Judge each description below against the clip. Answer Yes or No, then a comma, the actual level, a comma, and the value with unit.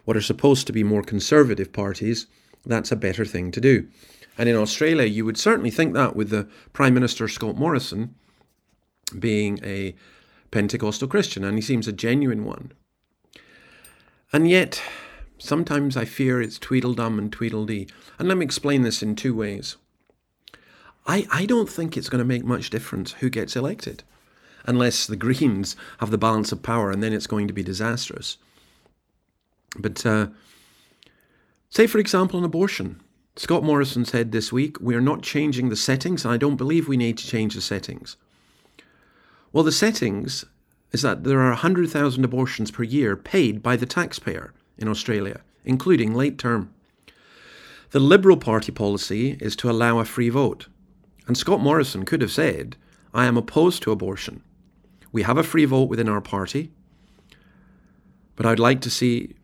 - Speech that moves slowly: No, average, 165 wpm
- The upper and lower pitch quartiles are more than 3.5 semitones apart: Yes, average, 4.6 semitones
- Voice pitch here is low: Yes, low, 120 Hz